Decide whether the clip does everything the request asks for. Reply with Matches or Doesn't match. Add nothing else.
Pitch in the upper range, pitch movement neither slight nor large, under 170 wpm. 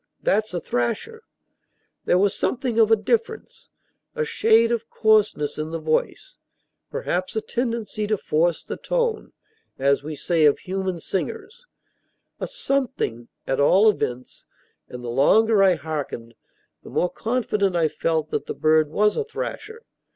Doesn't match